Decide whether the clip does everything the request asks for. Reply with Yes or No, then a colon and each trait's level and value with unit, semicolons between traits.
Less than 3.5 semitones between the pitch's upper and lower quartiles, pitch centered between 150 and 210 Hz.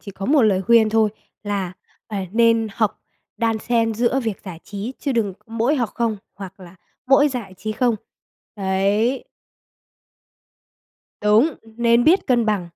No: average, 2.9 semitones; high, 225 Hz